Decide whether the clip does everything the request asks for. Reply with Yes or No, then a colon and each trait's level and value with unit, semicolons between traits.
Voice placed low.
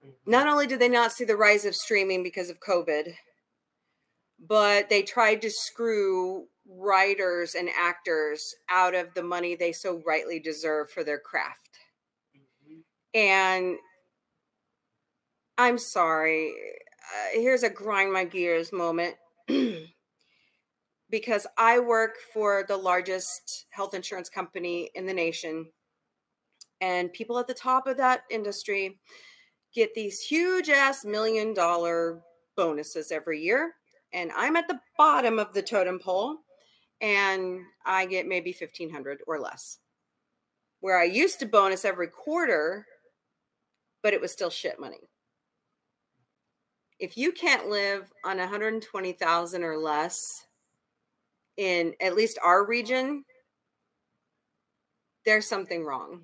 No: high, 195 Hz